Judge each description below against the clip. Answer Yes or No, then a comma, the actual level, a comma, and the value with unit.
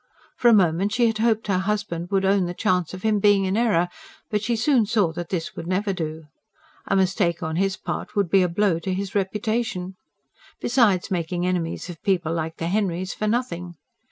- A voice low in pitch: No, high, 190 Hz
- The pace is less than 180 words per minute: No, fast, 205 wpm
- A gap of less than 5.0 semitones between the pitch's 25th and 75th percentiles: Yes, average, 3.3 semitones